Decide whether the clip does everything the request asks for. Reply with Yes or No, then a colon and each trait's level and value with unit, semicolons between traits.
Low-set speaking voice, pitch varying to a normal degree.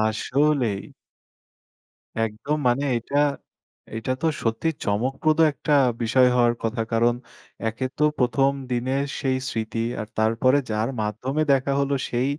Yes: low, 125 Hz; average, 3.5 semitones